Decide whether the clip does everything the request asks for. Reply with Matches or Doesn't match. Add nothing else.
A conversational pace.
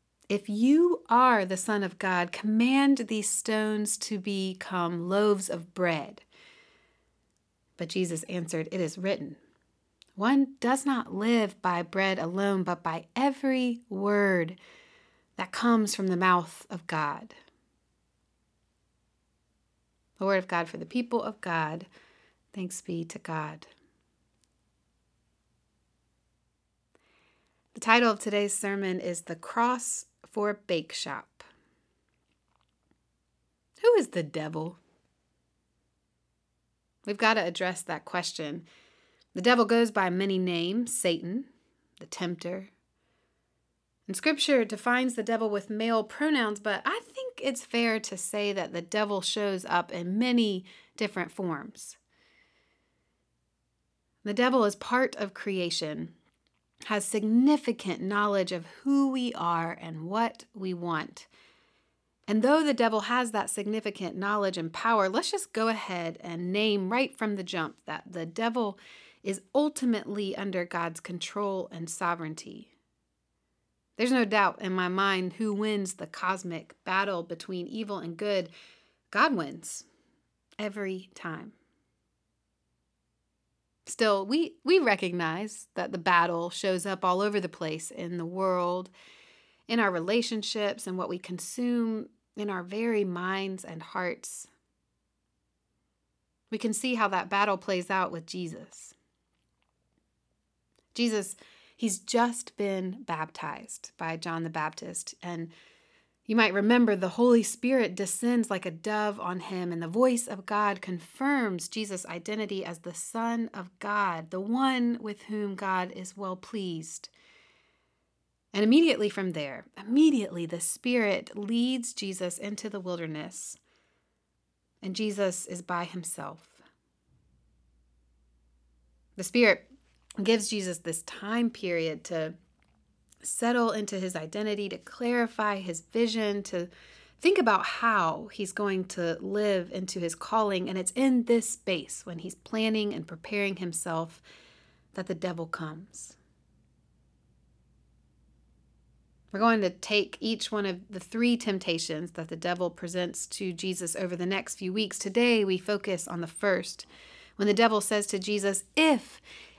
Doesn't match